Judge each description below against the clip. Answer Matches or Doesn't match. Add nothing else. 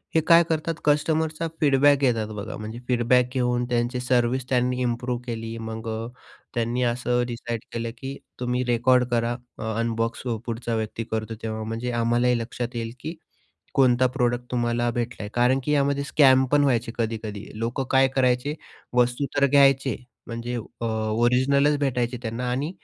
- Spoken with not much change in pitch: Matches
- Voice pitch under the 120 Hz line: Doesn't match